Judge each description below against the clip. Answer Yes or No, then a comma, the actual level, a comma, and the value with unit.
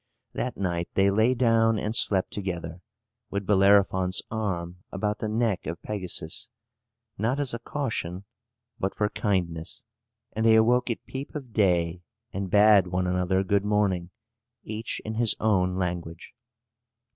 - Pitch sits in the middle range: No, low, 100 Hz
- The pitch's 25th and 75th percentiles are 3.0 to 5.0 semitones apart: Yes, average, 3.4 semitones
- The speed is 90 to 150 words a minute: Yes, average, 145 wpm